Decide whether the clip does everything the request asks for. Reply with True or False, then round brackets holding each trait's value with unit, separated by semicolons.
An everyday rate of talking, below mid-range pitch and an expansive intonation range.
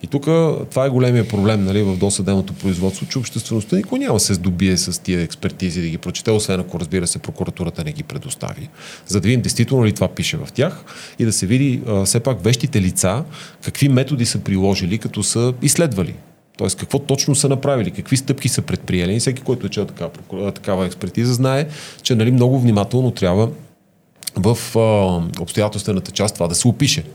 False (190 wpm; 115 Hz; 5.9 semitones)